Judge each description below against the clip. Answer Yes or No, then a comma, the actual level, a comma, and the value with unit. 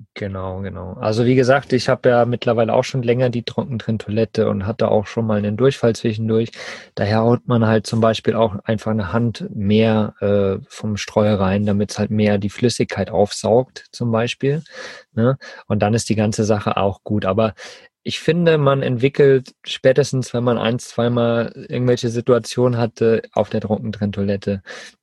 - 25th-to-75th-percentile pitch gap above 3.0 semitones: No, narrow, 2.6 semitones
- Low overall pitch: Yes, low, 115 Hz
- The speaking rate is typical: Yes, average, 170 wpm